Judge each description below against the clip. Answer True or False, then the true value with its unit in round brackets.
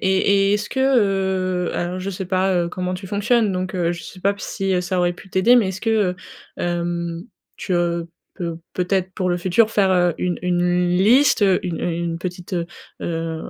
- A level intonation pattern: True (1.8 semitones)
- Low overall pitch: False (185 Hz)